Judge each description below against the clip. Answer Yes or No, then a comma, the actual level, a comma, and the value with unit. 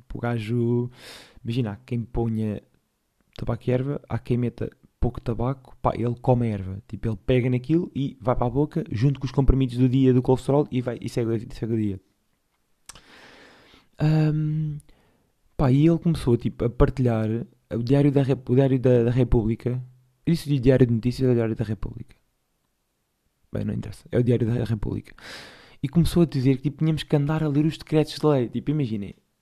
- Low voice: Yes, low, 125 Hz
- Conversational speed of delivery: No, fast, 195 wpm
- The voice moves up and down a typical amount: Yes, average, 3.3 semitones